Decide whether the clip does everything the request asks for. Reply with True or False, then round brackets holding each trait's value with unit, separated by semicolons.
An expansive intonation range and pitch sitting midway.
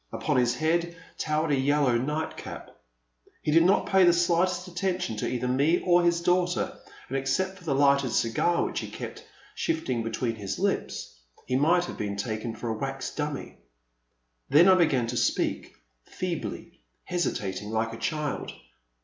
True (6.0 semitones; 150 Hz)